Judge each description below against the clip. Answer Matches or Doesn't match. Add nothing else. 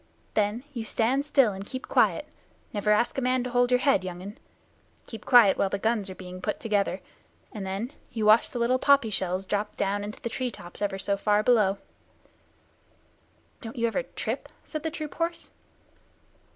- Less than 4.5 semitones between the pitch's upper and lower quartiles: Matches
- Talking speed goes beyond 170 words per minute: Matches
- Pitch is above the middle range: Matches